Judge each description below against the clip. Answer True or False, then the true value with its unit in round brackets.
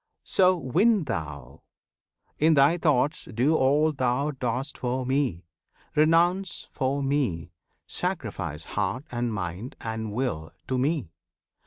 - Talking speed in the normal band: False (120 wpm)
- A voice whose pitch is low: True (130 Hz)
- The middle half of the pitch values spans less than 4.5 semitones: False (5.3 semitones)